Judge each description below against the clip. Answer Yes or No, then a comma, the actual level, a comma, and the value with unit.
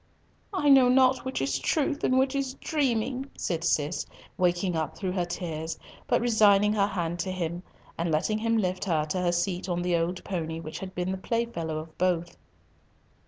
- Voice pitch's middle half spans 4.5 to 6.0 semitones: Yes, wide, 5.5 semitones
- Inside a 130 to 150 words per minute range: No, average, 190 wpm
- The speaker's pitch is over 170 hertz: Yes, medium, 185 Hz